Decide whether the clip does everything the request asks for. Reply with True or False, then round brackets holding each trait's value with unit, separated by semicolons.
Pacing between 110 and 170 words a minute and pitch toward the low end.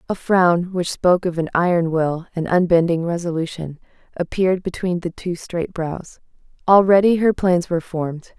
False (155 wpm; 175 Hz)